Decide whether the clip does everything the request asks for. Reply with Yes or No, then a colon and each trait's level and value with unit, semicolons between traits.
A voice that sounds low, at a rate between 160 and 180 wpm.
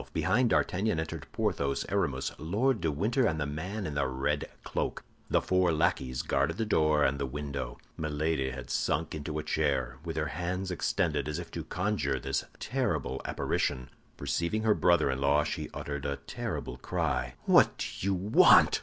Yes: very low, 75 Hz; average, 175 wpm